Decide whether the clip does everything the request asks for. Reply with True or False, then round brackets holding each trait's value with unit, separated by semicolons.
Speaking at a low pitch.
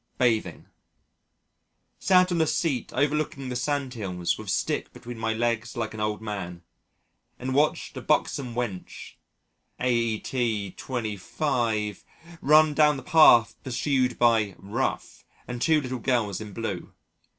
True (120 Hz)